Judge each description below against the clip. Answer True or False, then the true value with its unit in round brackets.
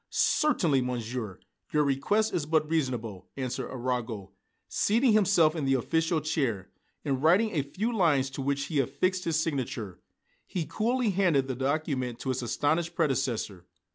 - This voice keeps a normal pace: True (150 wpm)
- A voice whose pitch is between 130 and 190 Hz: True (140 Hz)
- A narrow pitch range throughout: False (4.8 semitones)